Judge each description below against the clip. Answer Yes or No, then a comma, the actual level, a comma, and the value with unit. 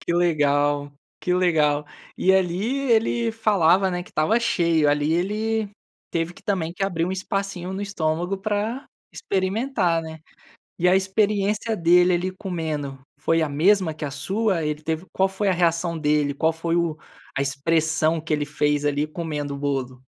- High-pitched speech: No, medium, 170 Hz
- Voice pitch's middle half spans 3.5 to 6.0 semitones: Yes, average, 4.0 semitones